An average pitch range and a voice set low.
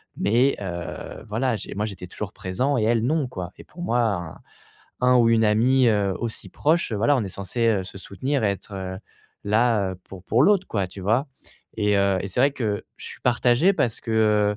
Yes: average, 4.1 semitones; low, 110 Hz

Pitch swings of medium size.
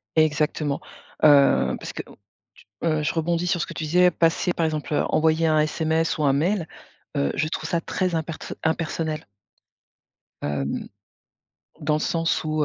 No: narrow, 1.4 semitones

